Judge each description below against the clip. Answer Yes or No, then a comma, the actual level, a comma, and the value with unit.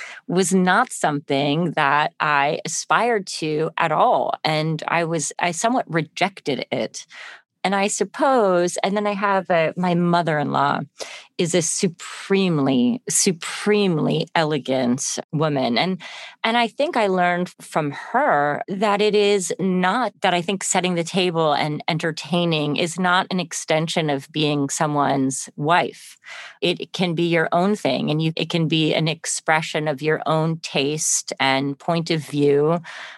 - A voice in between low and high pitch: Yes, medium, 170 Hz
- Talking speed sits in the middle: Yes, average, 145 wpm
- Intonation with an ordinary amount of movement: Yes, average, 3.5 semitones